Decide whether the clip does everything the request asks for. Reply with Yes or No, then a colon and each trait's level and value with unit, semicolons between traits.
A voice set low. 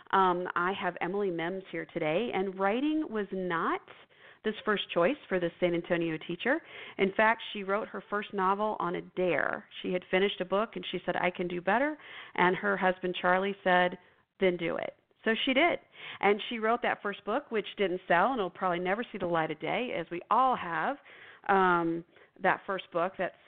No: medium, 185 Hz